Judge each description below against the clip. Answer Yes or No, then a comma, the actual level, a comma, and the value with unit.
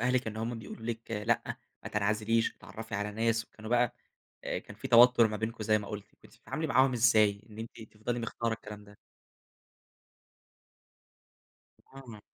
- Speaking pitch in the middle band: No, low, 110 Hz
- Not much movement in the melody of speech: Yes, narrow, 1.8 semitones